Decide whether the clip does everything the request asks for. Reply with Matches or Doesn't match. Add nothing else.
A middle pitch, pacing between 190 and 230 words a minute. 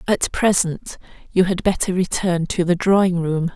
Doesn't match